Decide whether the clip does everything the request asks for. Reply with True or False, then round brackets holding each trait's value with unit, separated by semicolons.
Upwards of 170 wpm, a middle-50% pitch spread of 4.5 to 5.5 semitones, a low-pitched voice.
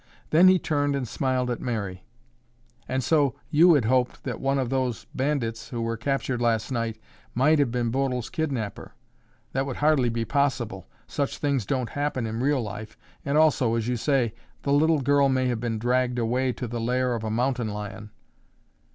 False (185 wpm; 3.3 semitones; 125 Hz)